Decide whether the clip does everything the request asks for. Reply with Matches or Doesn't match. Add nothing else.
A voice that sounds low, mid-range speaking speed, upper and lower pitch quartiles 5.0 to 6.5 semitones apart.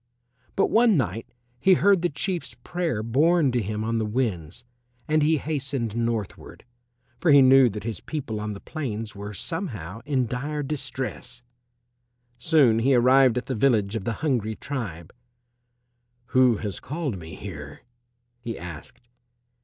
Matches